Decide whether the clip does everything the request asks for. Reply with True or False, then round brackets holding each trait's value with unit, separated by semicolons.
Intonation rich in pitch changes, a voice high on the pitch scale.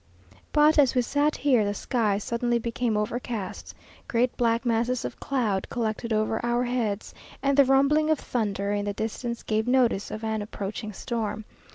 False (2.8 semitones; 235 Hz)